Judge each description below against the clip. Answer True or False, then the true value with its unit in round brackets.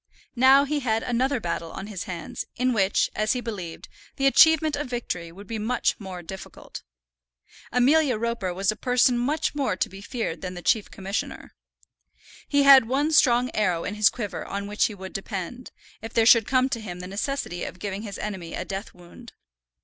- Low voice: False (220 Hz)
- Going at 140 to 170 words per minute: False (195 wpm)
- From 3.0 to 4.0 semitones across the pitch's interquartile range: False (4.9 semitones)